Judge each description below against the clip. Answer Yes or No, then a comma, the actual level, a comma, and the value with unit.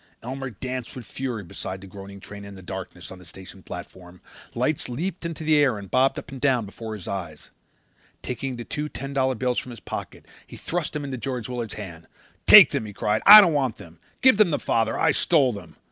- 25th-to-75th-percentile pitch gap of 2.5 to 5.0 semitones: No, wide, 5.6 semitones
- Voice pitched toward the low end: Yes, low, 120 Hz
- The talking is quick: Yes, fast, 225 wpm